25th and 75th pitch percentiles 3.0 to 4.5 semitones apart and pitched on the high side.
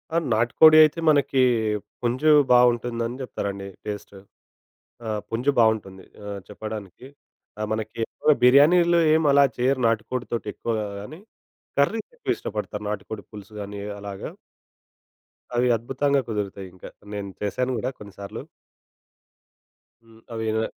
No: average, 4.2 semitones; low, 115 Hz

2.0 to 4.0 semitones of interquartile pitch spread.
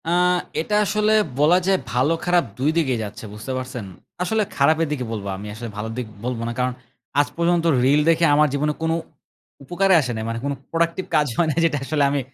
No: average, 4.9 semitones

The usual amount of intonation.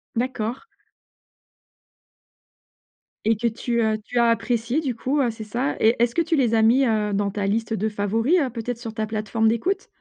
No: narrow, 2.2 semitones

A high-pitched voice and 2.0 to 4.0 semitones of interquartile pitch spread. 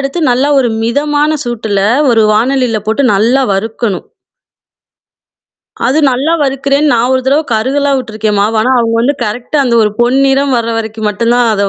Yes: high, 245 Hz; average, 3.7 semitones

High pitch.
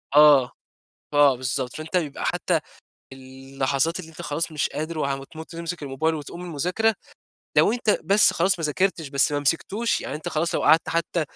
No: medium, 155 Hz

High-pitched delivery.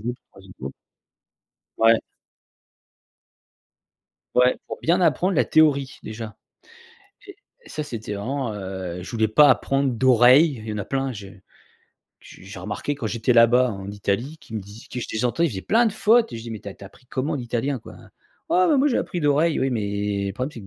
No: low, 120 Hz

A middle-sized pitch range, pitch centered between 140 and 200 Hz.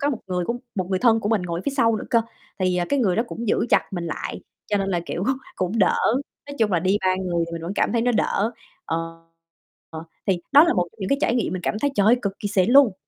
Yes: average, 4.4 semitones; high, 195 Hz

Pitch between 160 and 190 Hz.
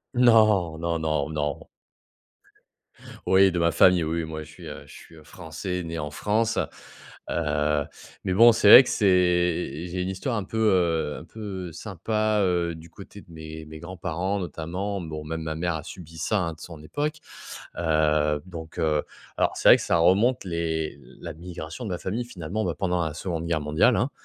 No: very low, 85 Hz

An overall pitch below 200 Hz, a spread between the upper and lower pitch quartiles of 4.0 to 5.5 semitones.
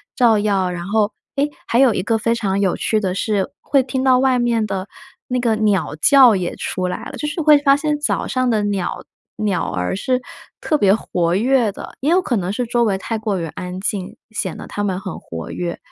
No: high, 215 Hz; average, 4.9 semitones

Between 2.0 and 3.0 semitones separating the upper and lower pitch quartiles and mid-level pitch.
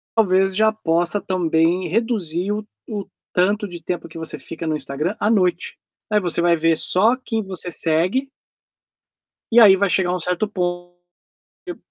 No: average, 3.6 semitones; medium, 180 Hz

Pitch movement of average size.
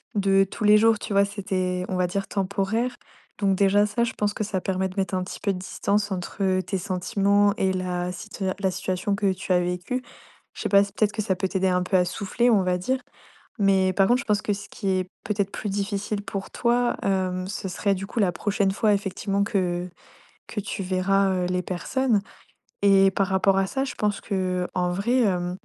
No: narrow, 1.8 semitones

